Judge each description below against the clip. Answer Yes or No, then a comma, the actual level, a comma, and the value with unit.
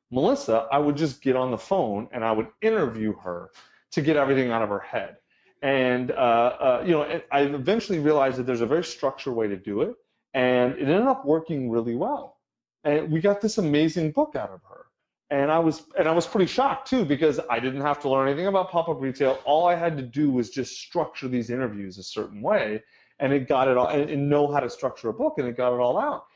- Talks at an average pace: No, fast, 235 wpm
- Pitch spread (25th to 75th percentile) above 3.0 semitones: Yes, average, 4.6 semitones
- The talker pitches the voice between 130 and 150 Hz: Yes, medium, 140 Hz